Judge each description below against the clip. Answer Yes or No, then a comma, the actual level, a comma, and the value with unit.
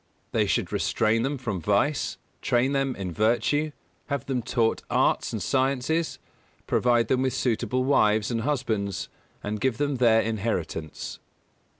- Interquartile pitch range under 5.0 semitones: Yes, average, 3.8 semitones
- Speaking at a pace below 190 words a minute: Yes, average, 140 wpm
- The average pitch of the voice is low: Yes, low, 120 Hz